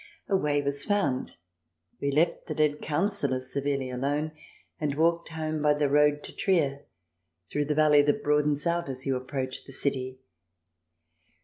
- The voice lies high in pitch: No, medium, 145 Hz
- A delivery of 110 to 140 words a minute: No, average, 155 wpm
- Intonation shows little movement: Yes, narrow, 1.8 semitones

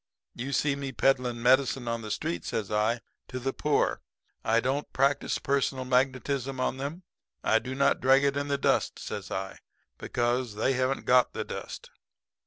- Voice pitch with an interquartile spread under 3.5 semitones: Yes, narrow, 2.5 semitones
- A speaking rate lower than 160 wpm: No, average, 175 wpm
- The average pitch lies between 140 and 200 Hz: No, low, 130 Hz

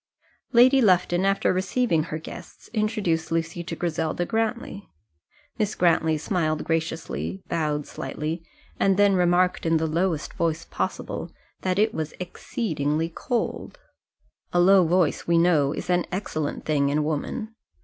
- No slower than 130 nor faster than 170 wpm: Yes, average, 140 wpm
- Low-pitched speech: No, medium, 170 Hz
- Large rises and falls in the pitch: No, average, 3.6 semitones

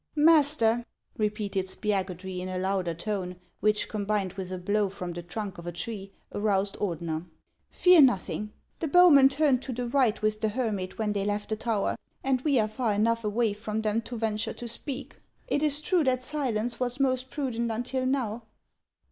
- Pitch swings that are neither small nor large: Yes, average, 4.3 semitones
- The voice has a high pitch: Yes, high, 215 Hz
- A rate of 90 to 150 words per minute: No, average, 185 wpm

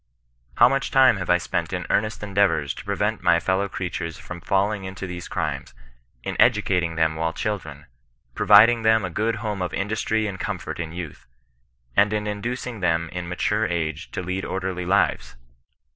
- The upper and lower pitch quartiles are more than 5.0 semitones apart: No, average, 3.5 semitones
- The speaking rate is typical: Yes, average, 175 wpm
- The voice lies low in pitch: Yes, very low, 95 Hz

